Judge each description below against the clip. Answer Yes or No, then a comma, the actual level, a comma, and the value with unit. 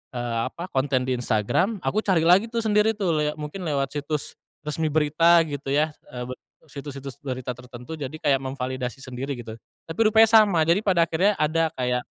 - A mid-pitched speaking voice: Yes, medium, 150 Hz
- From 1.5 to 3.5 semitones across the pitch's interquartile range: No, average, 4.9 semitones